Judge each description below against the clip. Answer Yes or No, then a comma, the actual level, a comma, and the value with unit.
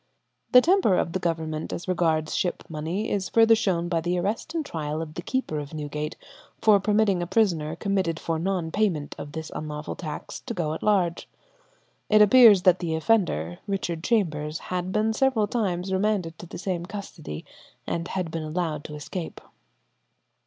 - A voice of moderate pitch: Yes, medium, 175 Hz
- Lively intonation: No, average, 4.4 semitones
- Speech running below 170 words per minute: No, average, 175 wpm